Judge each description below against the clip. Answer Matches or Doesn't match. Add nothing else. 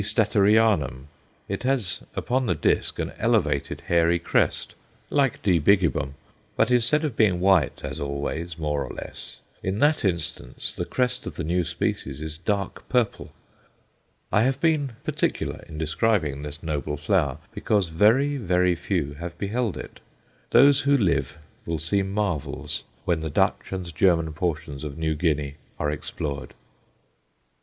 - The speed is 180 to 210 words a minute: Doesn't match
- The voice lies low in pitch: Matches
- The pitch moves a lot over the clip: Matches